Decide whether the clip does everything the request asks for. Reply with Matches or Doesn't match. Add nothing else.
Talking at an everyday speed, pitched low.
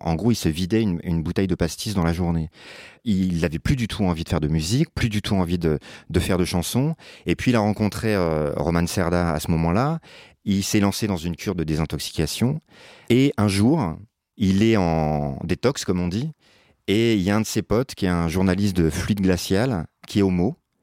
Doesn't match